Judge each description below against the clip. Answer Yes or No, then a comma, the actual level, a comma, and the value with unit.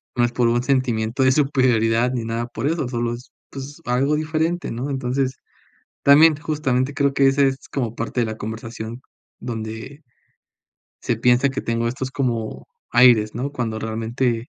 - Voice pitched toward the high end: No, low, 125 Hz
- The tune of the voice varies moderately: Yes, average, 3.0 semitones